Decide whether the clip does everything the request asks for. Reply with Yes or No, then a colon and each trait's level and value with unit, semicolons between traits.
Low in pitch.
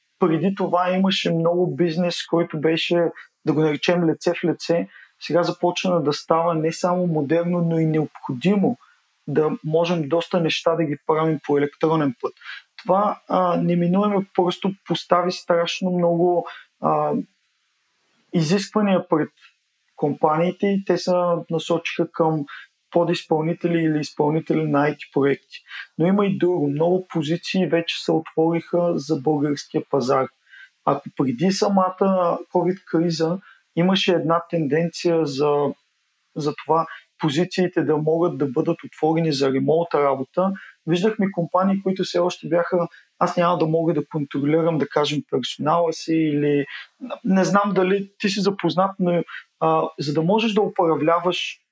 No: medium, 170 Hz